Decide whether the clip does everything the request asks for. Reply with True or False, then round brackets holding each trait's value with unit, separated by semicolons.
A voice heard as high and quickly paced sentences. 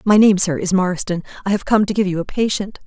True (195 Hz; 270 wpm)